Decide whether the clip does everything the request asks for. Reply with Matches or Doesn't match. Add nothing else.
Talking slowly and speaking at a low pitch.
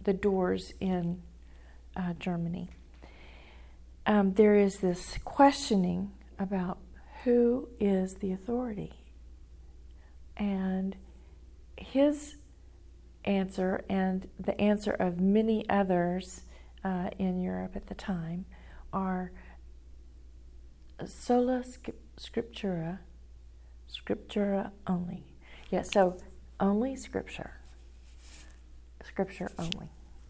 Doesn't match